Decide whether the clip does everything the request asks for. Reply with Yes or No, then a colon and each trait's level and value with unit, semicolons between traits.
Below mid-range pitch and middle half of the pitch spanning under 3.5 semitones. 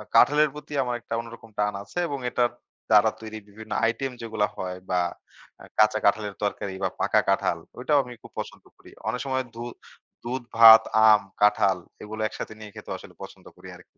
Yes: low, 110 Hz; average, 2.9 semitones